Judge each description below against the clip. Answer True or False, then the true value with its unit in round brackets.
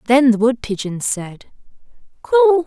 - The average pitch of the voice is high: True (260 Hz)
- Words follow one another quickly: False (135 wpm)